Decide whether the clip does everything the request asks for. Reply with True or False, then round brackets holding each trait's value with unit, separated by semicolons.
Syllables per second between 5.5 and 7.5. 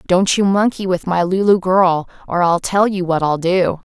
False (4.6 syllables/s)